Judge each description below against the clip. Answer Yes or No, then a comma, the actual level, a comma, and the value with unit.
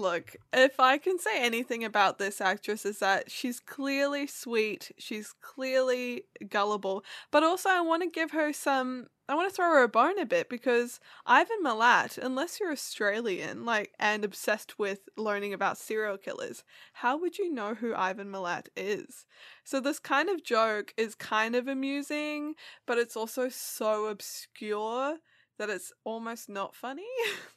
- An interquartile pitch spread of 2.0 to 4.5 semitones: No, wide, 5.4 semitones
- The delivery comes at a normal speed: Yes, average, 165 wpm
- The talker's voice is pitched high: Yes, high, 245 Hz